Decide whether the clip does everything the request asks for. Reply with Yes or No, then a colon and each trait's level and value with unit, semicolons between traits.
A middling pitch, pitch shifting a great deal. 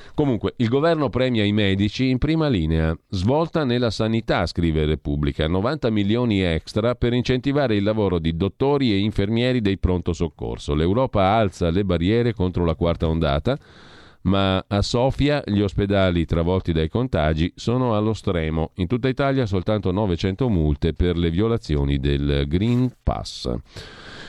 No: low, 100 Hz; wide, 6.2 semitones